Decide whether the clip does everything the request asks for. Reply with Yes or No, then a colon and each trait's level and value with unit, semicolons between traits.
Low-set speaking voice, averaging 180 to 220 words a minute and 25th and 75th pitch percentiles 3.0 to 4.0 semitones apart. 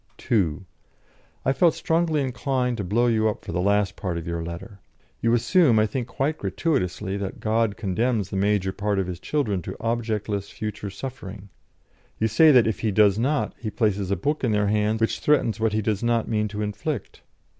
Yes: low, 110 Hz; average, 200 wpm; average, 3.4 semitones